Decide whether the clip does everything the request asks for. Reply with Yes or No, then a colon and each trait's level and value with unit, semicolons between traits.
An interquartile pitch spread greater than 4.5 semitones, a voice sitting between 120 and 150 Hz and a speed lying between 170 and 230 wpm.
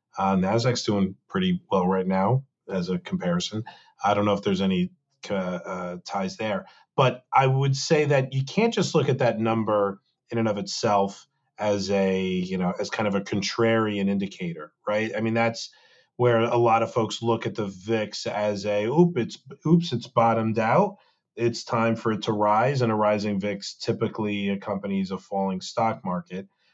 No: average, 4.9 semitones; low, 110 Hz; average, 185 wpm